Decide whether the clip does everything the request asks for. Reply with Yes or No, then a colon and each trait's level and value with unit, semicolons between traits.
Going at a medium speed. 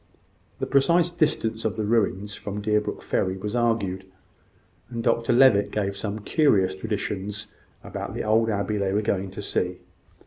Yes: average, 160 wpm